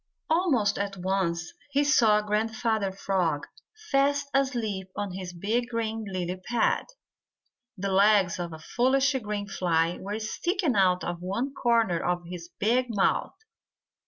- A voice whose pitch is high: Yes, high, 205 Hz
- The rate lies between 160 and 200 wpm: No, slow, 135 wpm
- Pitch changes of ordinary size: Yes, average, 4.6 semitones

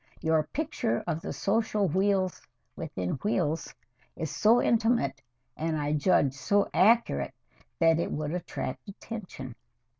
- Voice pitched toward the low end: No, medium, 170 Hz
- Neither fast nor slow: No, slow, 125 wpm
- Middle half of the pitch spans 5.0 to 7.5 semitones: Yes, average, 5.3 semitones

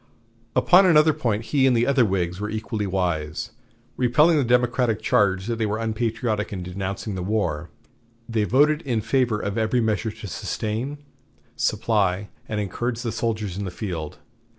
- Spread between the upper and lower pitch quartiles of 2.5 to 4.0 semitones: Yes, average, 3.6 semitones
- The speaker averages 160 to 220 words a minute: Yes, average, 165 wpm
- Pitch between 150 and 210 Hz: No, low, 110 Hz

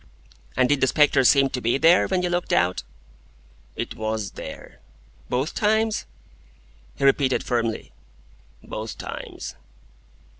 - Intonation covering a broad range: Yes, wide, 6.0 semitones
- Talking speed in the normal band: No, slow, 125 wpm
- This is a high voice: No, low, 135 Hz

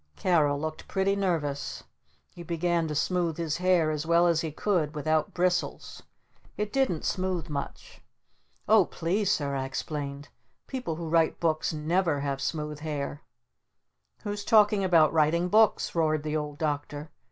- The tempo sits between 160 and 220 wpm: No, average, 150 wpm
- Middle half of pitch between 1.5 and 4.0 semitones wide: Yes, average, 3.2 semitones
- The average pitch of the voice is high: No, medium, 160 Hz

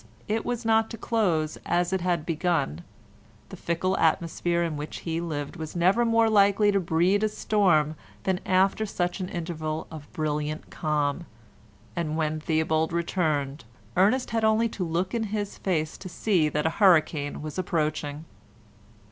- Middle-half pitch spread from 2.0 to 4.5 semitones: Yes, average, 4.1 semitones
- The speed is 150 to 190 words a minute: Yes, average, 160 wpm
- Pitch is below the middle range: No, medium, 170 Hz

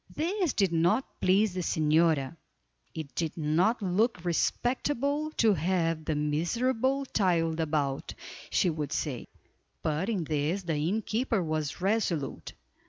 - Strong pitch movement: Yes, wide, 5.9 semitones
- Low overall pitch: No, medium, 175 Hz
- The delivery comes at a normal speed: No, slow, 125 wpm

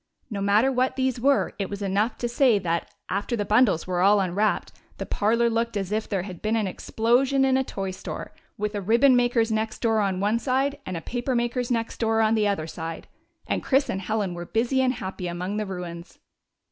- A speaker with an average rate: No, fast, 215 wpm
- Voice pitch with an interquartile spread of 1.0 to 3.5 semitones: No, average, 3.9 semitones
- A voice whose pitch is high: Yes, high, 215 Hz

